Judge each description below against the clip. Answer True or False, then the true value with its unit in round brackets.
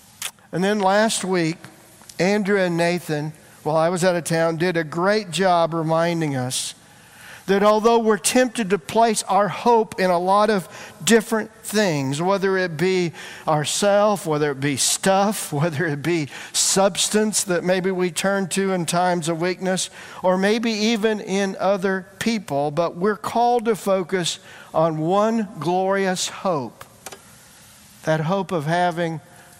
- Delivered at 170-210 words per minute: False (150 wpm)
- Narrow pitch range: False (3.5 semitones)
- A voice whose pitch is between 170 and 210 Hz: True (185 Hz)